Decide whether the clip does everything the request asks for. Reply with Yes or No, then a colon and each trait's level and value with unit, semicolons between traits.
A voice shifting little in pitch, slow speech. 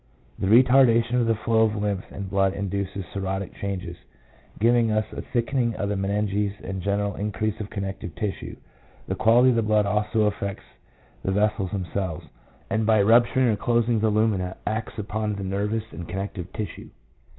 No: narrow, 2.2 semitones; average, 180 wpm